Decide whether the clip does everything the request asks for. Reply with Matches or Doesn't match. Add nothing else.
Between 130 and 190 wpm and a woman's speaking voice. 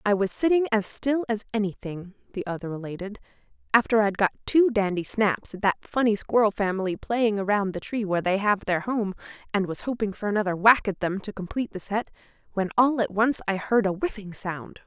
Doesn't match